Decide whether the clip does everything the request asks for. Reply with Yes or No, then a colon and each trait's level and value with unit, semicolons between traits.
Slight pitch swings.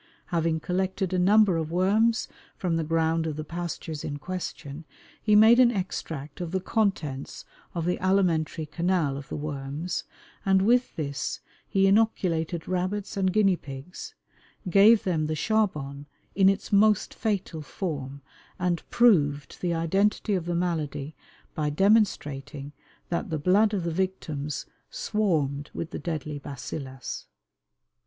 No: average, 4.3 semitones